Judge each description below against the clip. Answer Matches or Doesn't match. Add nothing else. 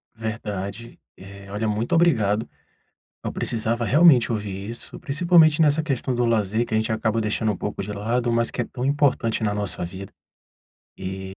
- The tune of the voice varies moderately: Matches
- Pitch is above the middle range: Doesn't match